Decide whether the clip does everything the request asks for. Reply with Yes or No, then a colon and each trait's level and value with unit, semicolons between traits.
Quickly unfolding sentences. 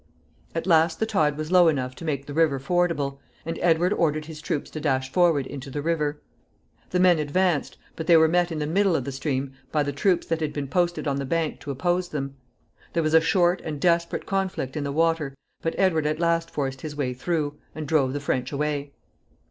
Yes: fast, 220 wpm